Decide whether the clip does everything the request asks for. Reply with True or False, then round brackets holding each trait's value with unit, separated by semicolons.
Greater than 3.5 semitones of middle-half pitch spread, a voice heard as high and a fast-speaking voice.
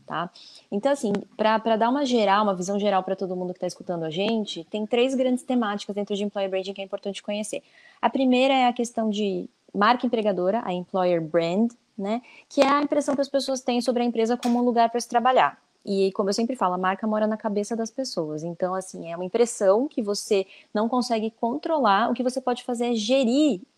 True (3.9 semitones; 225 Hz; 220 wpm)